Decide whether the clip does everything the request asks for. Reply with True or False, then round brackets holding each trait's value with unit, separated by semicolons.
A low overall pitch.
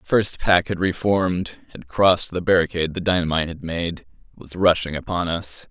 True (90 Hz)